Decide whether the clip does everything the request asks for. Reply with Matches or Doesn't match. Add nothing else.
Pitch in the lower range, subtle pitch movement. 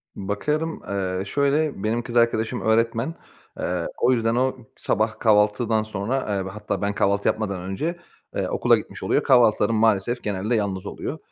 Doesn't match